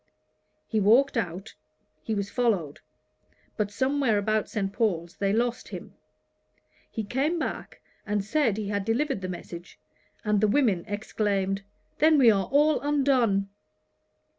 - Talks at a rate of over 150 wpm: No, average, 140 wpm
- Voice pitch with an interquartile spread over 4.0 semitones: Yes, average, 4.4 semitones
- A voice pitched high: Yes, high, 215 Hz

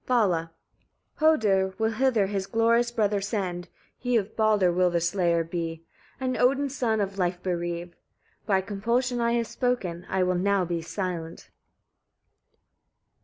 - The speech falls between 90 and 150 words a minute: Yes, average, 145 wpm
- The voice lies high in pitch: Yes, high, 195 Hz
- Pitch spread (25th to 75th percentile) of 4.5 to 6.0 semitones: Yes, average, 4.8 semitones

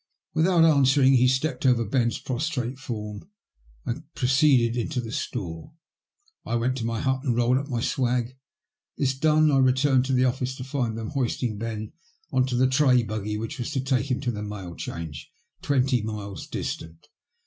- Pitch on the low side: Yes, low, 125 Hz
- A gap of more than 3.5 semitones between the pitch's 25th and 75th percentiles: No, average, 2.7 semitones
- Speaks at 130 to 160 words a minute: No, average, 175 wpm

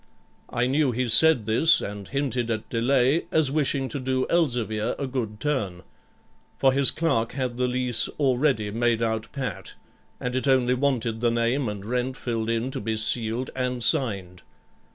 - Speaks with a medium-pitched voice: No, low, 125 Hz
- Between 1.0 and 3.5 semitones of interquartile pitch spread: Yes, average, 2.9 semitones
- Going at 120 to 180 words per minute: Yes, average, 170 wpm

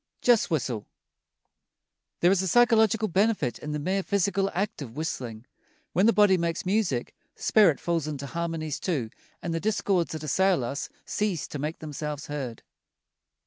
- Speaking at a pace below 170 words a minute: Yes, average, 160 wpm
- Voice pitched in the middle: Yes, medium, 170 Hz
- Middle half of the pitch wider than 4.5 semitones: Yes, average, 5.1 semitones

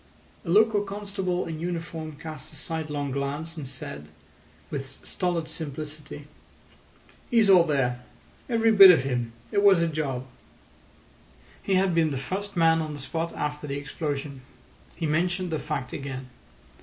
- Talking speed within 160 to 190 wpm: No, average, 150 wpm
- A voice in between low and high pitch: Yes, medium, 155 Hz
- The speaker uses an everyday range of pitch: Yes, average, 4.1 semitones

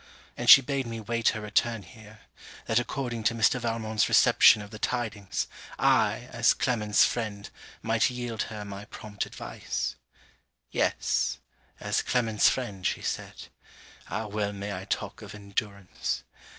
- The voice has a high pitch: No, low, 110 Hz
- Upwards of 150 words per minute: No, average, 145 wpm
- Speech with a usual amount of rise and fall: No, narrow, 2.2 semitones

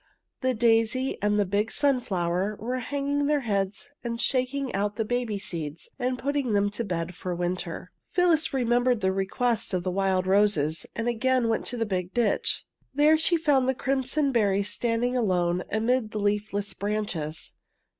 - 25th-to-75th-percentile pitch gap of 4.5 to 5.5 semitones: Yes, average, 4.8 semitones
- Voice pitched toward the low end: No, high, 220 Hz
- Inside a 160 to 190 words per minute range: Yes, average, 175 wpm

